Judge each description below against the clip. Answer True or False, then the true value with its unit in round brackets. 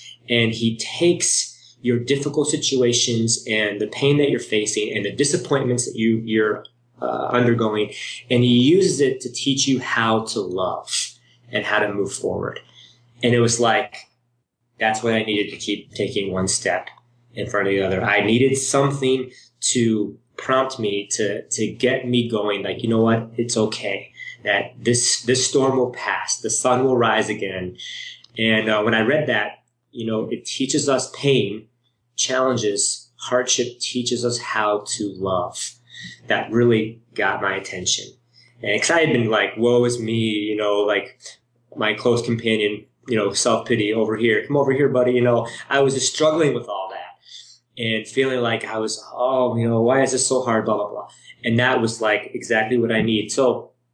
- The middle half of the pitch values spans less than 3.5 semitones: True (2.7 semitones)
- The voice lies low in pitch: True (120 Hz)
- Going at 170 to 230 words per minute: True (180 wpm)